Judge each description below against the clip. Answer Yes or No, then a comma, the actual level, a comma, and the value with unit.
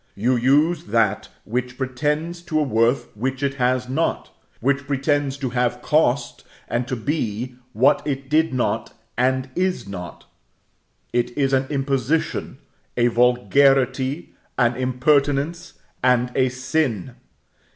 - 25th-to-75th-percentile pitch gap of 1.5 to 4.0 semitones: Yes, narrow, 2.6 semitones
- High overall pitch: No, low, 130 Hz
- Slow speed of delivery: Yes, slow, 130 wpm